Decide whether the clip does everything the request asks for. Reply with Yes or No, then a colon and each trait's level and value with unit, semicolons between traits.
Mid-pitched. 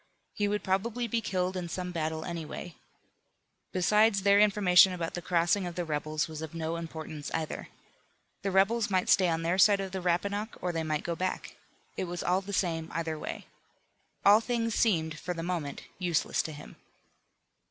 Yes: medium, 180 Hz